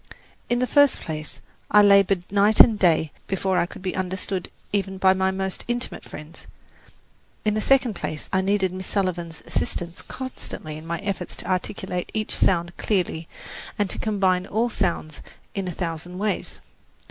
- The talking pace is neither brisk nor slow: Yes, average, 165 wpm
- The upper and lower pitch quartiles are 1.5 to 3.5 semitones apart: Yes, average, 2.8 semitones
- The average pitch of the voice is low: No, high, 190 Hz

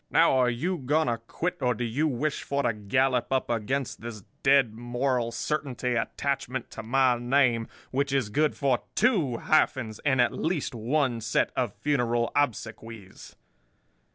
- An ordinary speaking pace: Yes, average, 155 wpm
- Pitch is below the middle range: Yes, low, 125 Hz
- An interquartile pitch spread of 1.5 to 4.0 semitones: Yes, average, 3.1 semitones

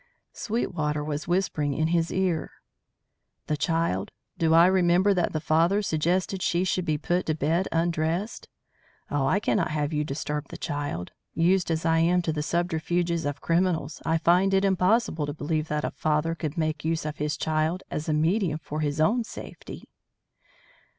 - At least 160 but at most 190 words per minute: Yes, average, 175 wpm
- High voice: No, medium, 165 Hz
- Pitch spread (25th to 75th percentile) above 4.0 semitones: No, average, 2.7 semitones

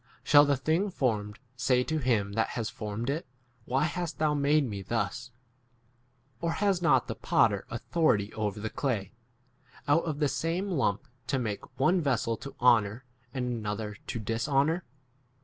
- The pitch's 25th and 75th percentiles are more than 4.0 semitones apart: Yes, wide, 5.5 semitones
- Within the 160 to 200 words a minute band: Yes, average, 165 wpm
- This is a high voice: No, low, 130 Hz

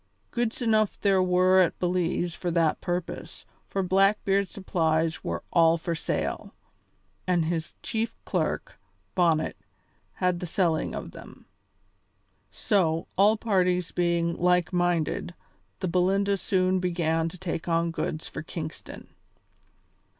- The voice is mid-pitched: Yes, medium, 180 Hz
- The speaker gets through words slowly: Yes, slow, 125 wpm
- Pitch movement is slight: Yes, narrow, 2.2 semitones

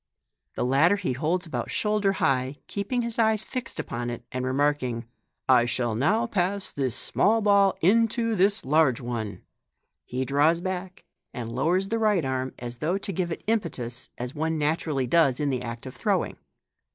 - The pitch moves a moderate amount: No, wide, 7.6 semitones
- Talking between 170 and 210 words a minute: Yes, average, 175 wpm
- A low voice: No, medium, 155 Hz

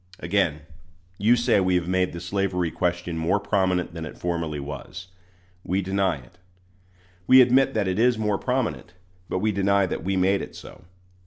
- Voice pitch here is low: Yes, very low, 95 Hz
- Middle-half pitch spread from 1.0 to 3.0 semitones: Yes, narrow, 2.6 semitones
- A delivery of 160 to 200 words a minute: Yes, average, 175 wpm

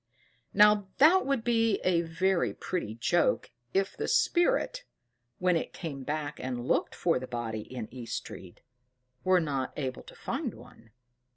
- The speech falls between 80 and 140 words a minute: No, average, 150 wpm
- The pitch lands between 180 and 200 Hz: No, medium, 170 Hz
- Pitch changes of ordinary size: No, wide, 8.0 semitones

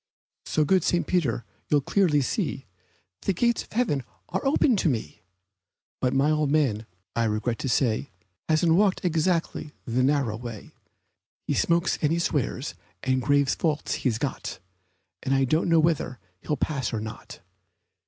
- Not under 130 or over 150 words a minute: No, average, 165 wpm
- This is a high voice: No, medium, 145 Hz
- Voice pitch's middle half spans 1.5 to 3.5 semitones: No, average, 4.8 semitones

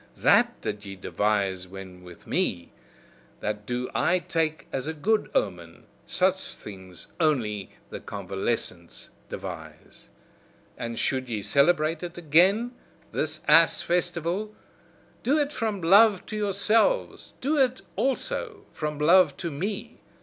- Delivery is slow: Yes, slow, 130 wpm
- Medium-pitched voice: Yes, medium, 155 Hz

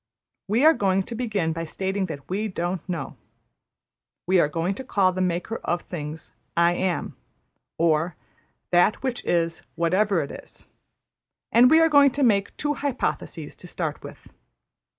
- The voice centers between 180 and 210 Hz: Yes, medium, 185 Hz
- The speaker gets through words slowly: No, average, 160 wpm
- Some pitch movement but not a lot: Yes, average, 4.9 semitones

